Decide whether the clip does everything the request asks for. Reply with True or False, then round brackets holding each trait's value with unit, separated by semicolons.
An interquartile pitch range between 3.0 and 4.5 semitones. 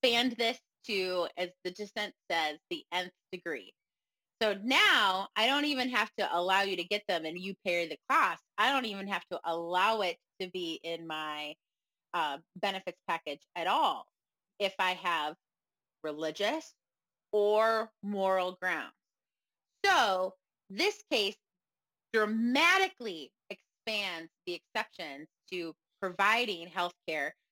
True (4.0 semitones)